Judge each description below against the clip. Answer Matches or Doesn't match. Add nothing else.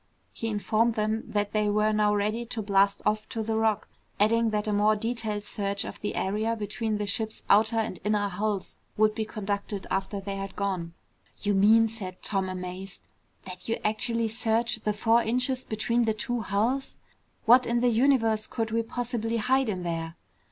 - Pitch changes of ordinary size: Doesn't match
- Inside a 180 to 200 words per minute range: Matches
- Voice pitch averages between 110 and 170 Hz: Doesn't match